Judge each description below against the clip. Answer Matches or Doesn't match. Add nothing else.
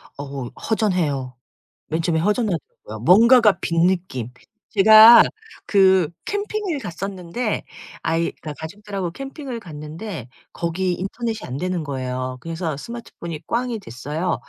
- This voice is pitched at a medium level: Matches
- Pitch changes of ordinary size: Doesn't match